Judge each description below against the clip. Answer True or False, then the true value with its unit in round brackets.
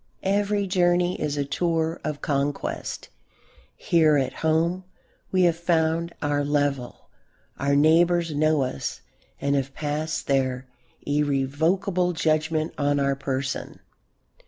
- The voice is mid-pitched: True (155 Hz)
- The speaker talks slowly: True (115 wpm)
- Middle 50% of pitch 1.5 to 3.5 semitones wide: True (3.2 semitones)